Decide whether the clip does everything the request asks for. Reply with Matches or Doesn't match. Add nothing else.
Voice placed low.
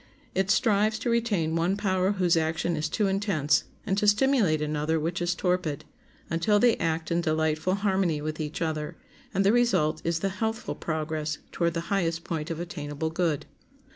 Doesn't match